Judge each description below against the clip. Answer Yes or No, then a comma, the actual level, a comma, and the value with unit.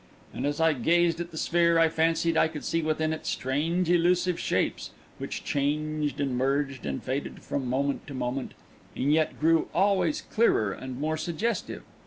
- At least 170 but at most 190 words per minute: Yes, average, 175 wpm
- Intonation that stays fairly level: No, average, 3.2 semitones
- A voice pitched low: No, medium, 155 Hz